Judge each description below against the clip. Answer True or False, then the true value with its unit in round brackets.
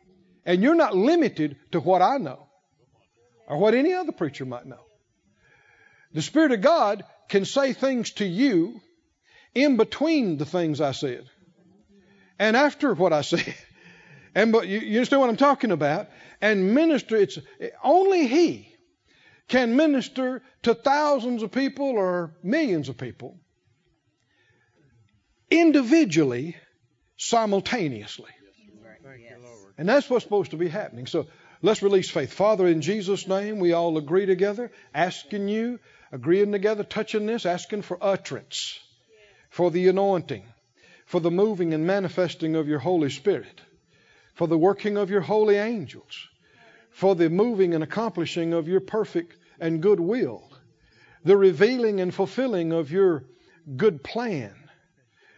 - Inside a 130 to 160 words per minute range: True (140 wpm)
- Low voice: False (195 Hz)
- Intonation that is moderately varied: False (6.3 semitones)